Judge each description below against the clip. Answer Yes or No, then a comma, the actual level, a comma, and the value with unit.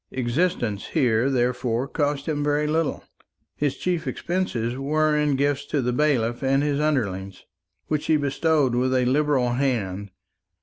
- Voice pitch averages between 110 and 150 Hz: Yes, low, 135 Hz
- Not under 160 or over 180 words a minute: No, average, 145 wpm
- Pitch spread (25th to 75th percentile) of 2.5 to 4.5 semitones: Yes, average, 3.6 semitones